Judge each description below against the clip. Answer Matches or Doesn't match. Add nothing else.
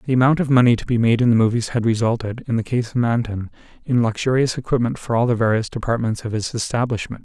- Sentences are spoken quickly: Matches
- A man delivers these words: Matches